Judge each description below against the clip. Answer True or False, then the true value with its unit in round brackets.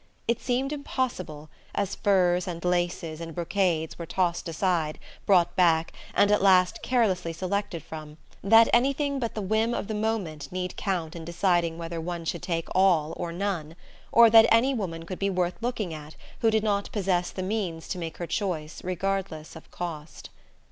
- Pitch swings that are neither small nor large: True (3.7 semitones)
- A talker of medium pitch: True (180 Hz)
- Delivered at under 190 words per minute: True (175 wpm)